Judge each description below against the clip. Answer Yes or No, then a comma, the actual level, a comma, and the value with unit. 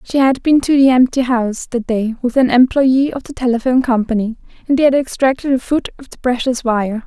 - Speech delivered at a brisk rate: Yes, fast, 220 wpm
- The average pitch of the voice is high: Yes, very high, 250 Hz